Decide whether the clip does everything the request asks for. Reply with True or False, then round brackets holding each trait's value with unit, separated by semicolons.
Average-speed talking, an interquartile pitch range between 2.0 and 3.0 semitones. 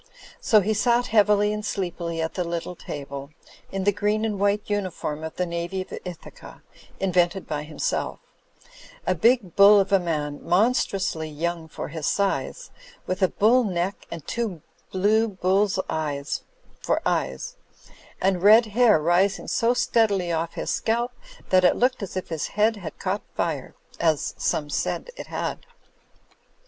False (155 wpm; 3.9 semitones)